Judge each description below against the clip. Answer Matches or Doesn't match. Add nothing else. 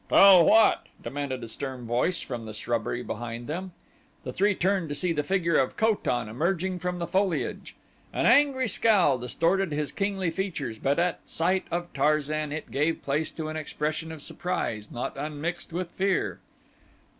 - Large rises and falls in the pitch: Doesn't match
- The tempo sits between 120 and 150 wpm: Doesn't match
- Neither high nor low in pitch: Matches